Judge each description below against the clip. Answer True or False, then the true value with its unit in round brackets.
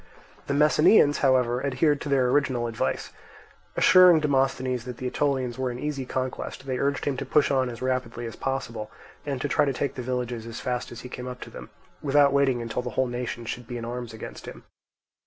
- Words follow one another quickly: True (210 wpm)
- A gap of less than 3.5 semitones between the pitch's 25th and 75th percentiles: True (2.4 semitones)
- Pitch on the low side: True (130 Hz)